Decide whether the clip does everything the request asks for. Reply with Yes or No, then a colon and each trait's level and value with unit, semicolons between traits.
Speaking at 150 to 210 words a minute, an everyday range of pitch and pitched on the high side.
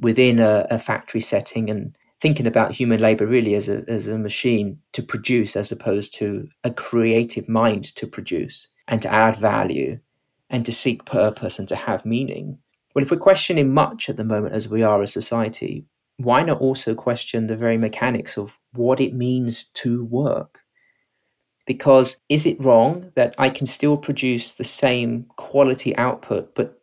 No: average, 175 wpm; average, 3.2 semitones; low, 120 Hz